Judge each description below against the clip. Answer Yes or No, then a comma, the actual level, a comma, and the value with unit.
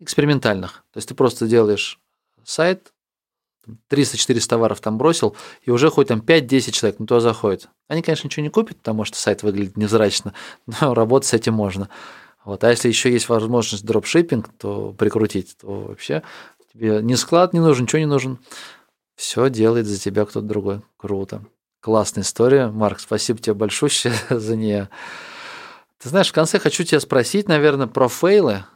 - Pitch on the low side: Yes, low, 115 Hz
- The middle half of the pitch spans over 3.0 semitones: Yes, average, 5.3 semitones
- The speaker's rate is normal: No, fast, 165 wpm